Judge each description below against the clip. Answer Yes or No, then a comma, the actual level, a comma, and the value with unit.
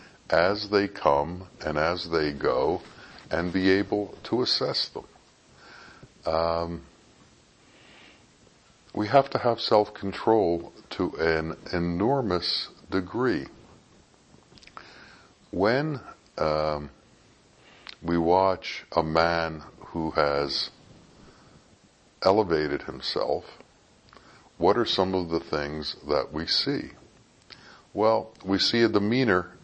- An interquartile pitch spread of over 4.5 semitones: No, average, 3.9 semitones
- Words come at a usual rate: No, slow, 95 wpm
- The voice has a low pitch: Yes, very low, 85 Hz